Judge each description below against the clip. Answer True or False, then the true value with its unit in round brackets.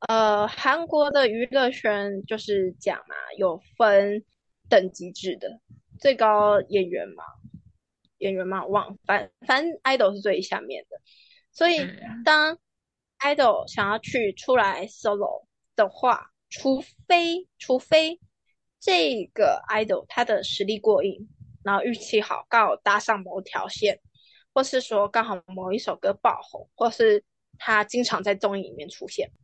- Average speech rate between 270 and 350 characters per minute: False (220 characters per minute)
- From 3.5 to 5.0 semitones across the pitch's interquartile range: False (5.4 semitones)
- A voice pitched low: False (220 Hz)